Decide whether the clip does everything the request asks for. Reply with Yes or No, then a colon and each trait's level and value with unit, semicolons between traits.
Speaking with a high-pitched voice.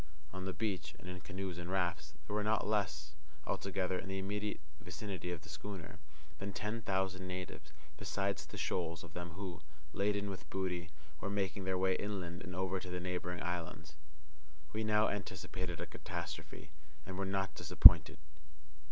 No: very low, 95 Hz